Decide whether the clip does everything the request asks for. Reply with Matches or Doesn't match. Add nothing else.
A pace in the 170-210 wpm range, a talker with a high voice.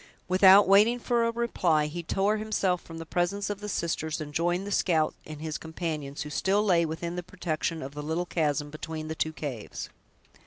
Doesn't match